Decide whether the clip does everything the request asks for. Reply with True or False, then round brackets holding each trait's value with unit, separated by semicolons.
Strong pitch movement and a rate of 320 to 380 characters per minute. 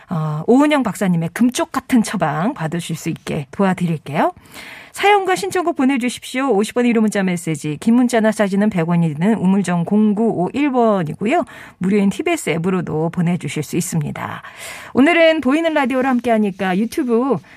True (7.0 semitones; 345 characters per minute)